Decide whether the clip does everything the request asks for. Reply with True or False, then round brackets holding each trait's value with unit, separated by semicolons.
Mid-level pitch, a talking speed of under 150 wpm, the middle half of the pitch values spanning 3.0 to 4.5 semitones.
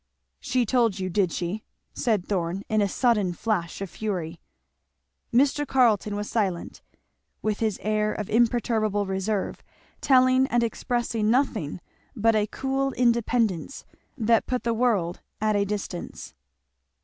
False (215 Hz; 135 wpm; 3.4 semitones)